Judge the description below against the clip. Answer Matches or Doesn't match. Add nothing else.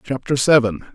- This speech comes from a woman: Doesn't match